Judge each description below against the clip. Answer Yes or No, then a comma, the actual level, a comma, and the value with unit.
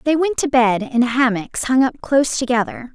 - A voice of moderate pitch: No, high, 245 Hz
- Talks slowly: No, fast, 205 wpm